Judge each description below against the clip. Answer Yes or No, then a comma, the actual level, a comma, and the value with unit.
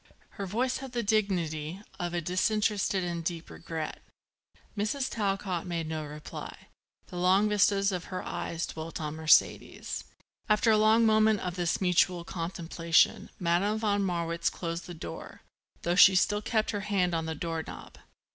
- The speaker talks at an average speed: Yes, average, 155 wpm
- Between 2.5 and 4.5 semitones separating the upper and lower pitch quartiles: Yes, average, 3.7 semitones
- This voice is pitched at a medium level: Yes, medium, 180 Hz